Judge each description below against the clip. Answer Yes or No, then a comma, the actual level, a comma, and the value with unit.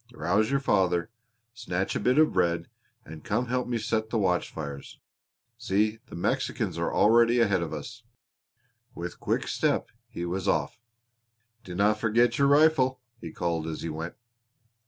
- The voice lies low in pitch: Yes, low, 105 Hz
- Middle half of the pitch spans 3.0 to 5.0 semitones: No, wide, 5.5 semitones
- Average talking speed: Yes, average, 160 wpm